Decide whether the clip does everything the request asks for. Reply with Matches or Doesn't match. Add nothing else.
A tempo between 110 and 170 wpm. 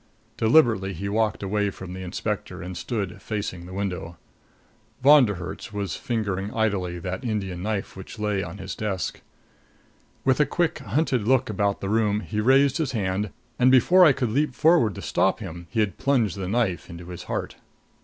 Doesn't match